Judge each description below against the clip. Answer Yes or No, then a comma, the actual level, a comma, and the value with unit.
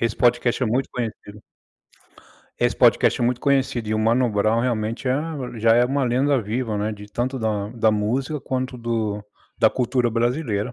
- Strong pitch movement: No, average, 2.8 semitones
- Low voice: Yes, low, 120 Hz